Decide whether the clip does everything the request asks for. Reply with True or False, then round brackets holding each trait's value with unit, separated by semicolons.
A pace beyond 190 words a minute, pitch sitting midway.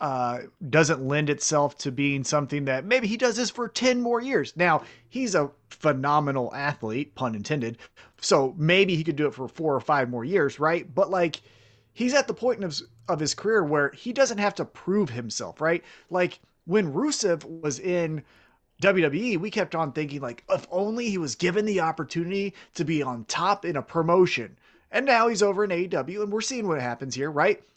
True (200 wpm; 165 Hz)